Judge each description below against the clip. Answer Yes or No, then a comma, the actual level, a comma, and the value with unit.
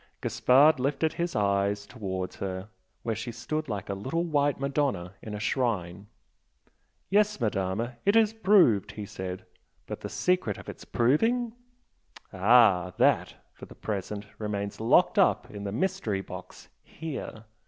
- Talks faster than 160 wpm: No, average, 150 wpm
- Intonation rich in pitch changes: Yes, wide, 6.7 semitones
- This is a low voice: Yes, low, 115 Hz